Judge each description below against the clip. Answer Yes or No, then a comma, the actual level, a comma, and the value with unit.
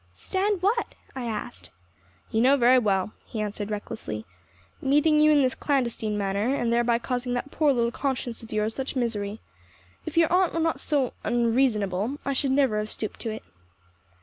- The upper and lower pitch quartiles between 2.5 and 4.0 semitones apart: No, average, 4.6 semitones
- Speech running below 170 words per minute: No, average, 175 wpm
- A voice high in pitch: Yes, high, 240 Hz